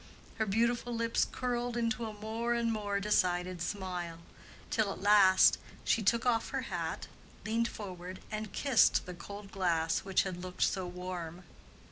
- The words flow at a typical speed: Yes, average, 155 wpm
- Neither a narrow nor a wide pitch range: Yes, average, 3.9 semitones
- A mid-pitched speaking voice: No, high, 205 Hz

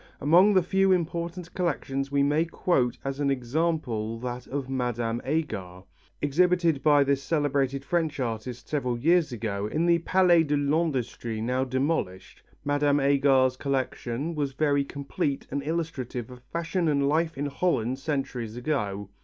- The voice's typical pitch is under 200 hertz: Yes, medium, 140 Hz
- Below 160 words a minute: Yes, average, 145 wpm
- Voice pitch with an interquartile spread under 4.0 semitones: No, average, 4.3 semitones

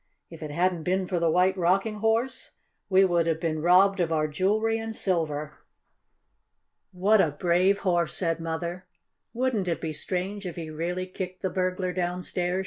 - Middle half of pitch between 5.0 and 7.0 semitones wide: No, narrow, 2.4 semitones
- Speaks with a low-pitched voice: No, medium, 180 Hz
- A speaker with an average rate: Yes, average, 170 wpm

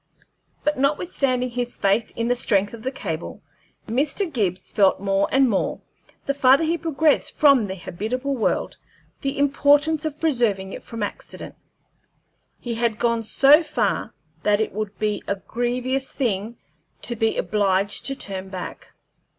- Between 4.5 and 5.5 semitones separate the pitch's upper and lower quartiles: Yes, average, 5.1 semitones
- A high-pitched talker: Yes, high, 240 Hz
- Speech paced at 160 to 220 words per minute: No, average, 150 wpm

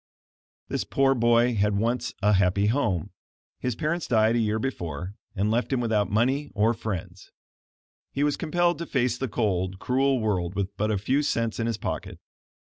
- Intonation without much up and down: No, average, 4.1 semitones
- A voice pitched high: No, low, 115 Hz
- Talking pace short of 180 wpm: No, average, 185 wpm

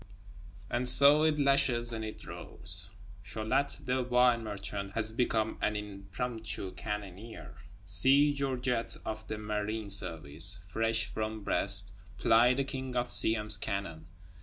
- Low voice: Yes, low, 110 Hz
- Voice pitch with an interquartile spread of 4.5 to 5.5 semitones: No, average, 3.8 semitones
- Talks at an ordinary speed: No, slow, 130 wpm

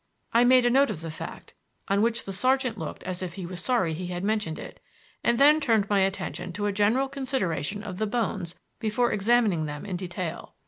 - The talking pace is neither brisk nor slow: No, fast, 215 wpm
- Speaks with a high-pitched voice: Yes, high, 205 Hz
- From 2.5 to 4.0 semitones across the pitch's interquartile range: No, average, 4.9 semitones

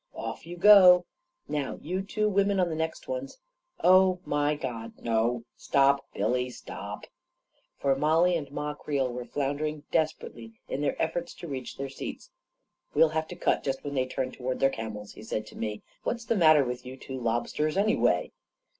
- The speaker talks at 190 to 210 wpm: Yes, average, 195 wpm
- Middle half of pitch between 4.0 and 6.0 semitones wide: Yes, average, 5.3 semitones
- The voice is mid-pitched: Yes, medium, 145 Hz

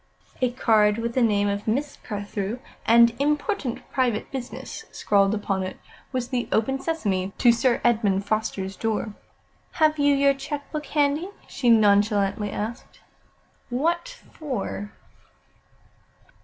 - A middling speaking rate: No, slow, 130 wpm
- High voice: Yes, high, 235 Hz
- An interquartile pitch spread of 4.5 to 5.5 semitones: Yes, average, 5.2 semitones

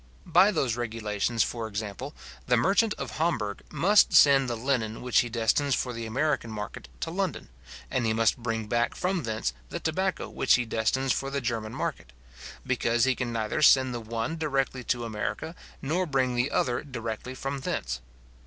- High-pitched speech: No, low, 125 Hz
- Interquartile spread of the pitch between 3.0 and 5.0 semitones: Yes, average, 3.8 semitones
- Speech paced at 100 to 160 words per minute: No, average, 180 wpm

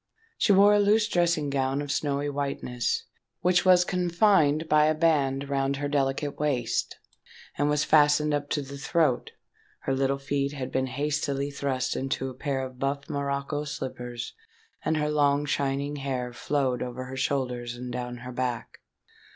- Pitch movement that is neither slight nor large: No, narrow, 2.1 semitones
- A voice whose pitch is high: No, medium, 140 Hz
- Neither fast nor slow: Yes, average, 165 wpm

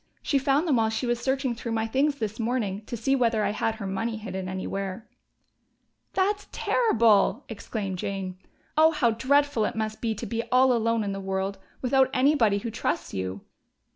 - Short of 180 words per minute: No, average, 185 wpm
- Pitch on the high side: Yes, high, 225 Hz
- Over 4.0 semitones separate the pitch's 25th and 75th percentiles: Yes, average, 4.6 semitones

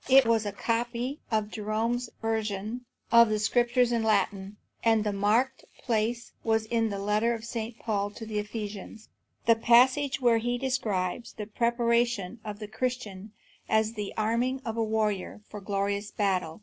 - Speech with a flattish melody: Yes, narrow, 2.3 semitones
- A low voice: No, high, 220 Hz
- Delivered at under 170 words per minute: Yes, average, 160 wpm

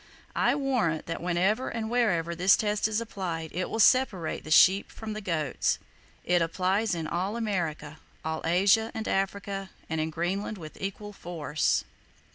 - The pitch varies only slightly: No, average, 4.3 semitones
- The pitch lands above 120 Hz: Yes, high, 190 Hz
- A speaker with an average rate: Yes, average, 160 wpm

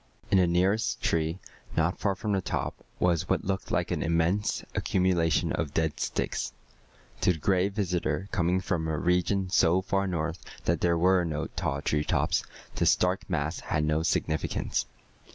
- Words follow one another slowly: No, average, 165 wpm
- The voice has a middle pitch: No, very low, 90 Hz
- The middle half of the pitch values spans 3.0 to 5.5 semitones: No, narrow, 2.6 semitones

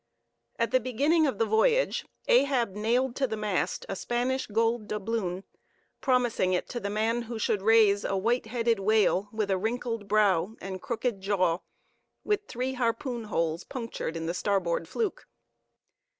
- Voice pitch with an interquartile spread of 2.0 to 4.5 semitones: Yes, average, 3.7 semitones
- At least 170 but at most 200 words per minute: No, average, 160 wpm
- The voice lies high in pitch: Yes, high, 220 Hz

